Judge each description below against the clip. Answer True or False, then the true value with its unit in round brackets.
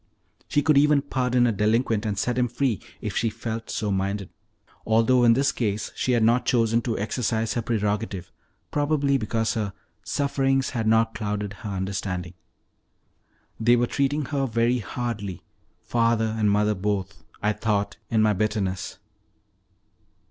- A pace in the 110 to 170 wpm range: True (150 wpm)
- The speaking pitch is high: False (115 Hz)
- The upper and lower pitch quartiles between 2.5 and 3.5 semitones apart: True (3.0 semitones)